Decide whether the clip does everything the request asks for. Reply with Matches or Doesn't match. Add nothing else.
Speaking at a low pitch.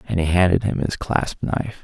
Matches